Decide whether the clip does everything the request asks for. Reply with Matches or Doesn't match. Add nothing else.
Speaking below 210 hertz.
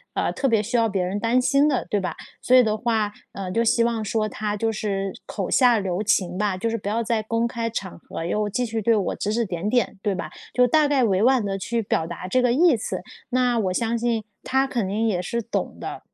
Doesn't match